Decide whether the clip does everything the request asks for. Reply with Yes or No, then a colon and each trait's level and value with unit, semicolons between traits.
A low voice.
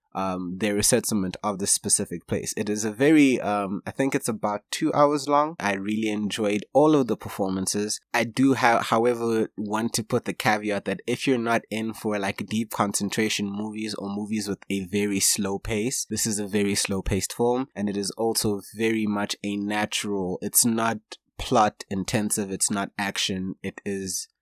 Yes: low, 105 Hz